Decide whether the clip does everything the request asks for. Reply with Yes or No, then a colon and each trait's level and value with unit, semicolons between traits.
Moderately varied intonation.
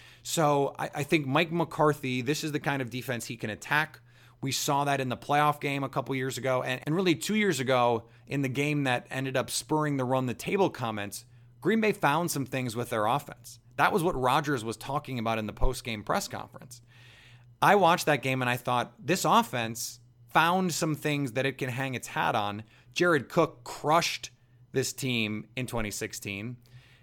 Yes: average, 3.6 semitones